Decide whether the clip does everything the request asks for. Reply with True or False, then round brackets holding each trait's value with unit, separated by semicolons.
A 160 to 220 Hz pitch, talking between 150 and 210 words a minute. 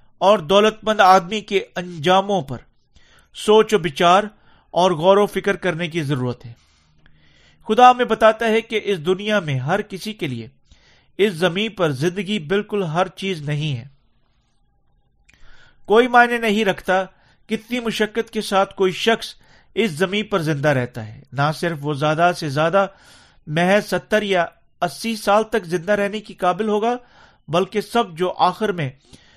True (190 Hz; 155 wpm)